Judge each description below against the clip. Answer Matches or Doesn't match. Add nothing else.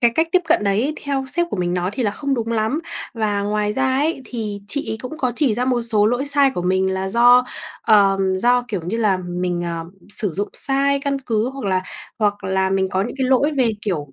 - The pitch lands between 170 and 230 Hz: Matches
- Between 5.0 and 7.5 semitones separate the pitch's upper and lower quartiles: Matches